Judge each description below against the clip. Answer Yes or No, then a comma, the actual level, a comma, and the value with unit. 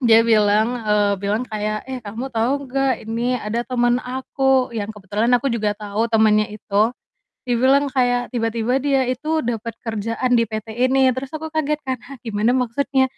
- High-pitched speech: Yes, high, 240 Hz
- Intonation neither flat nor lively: Yes, average, 3.2 semitones